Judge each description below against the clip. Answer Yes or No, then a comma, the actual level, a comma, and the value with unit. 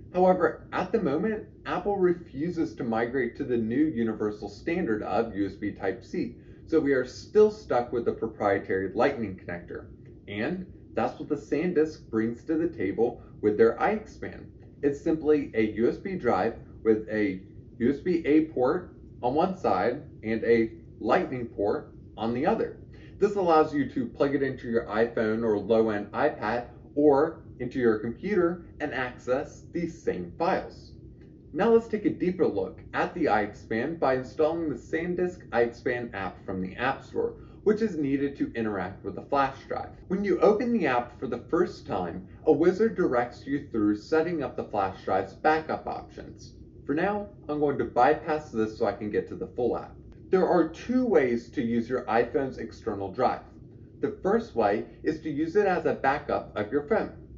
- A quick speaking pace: No, average, 175 wpm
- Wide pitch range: Yes, wide, 6.0 semitones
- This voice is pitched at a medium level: No, low, 130 Hz